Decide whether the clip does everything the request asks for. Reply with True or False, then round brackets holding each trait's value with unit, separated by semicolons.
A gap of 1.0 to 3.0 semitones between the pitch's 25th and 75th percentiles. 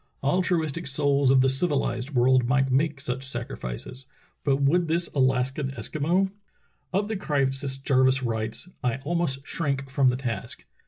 True (2.7 semitones)